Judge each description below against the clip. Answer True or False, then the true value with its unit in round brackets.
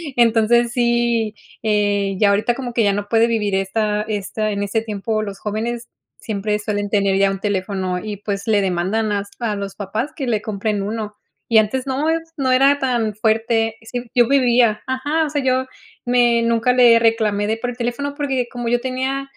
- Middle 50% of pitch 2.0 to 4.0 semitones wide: True (2.8 semitones)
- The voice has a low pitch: False (225 Hz)